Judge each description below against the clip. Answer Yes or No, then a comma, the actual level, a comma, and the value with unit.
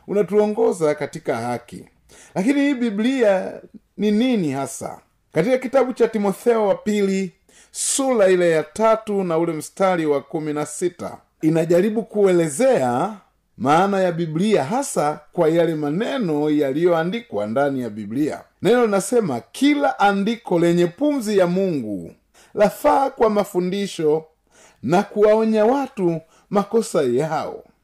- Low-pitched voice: No, high, 195 Hz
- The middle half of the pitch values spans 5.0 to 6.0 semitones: Yes, wide, 5.6 semitones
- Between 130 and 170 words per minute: No, average, 110 wpm